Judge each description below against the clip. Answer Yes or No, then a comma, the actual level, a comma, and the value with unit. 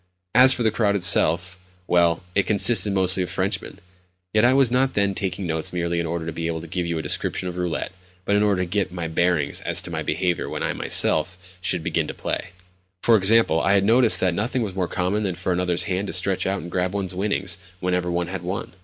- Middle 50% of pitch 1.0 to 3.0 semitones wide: Yes, narrow, 2.6 semitones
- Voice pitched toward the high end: No, very low, 90 Hz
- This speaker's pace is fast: Yes, fast, 230 wpm